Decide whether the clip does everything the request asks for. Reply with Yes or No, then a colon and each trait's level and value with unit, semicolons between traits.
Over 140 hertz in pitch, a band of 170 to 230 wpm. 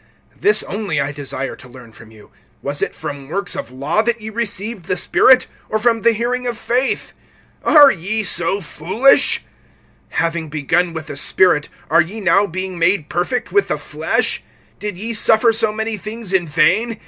Yes: high, 190 Hz; average, 180 wpm